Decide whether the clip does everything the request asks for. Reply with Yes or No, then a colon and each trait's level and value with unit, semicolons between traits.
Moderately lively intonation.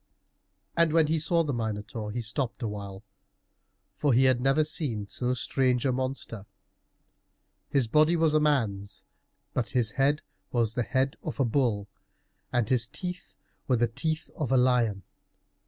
Yes: average, 4.6 semitones